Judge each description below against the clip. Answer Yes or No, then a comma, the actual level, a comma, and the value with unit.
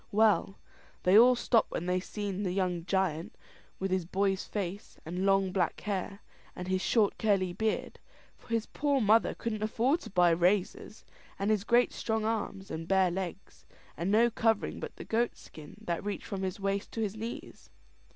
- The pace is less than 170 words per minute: No, average, 180 wpm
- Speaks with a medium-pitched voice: No, high, 195 Hz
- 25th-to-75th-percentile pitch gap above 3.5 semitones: No, average, 3.0 semitones